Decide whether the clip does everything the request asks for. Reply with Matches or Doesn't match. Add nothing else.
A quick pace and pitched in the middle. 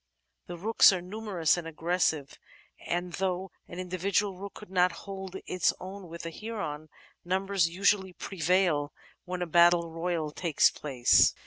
Doesn't match